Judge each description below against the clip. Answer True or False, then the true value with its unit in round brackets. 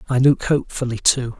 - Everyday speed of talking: True (175 wpm)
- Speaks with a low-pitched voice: True (130 Hz)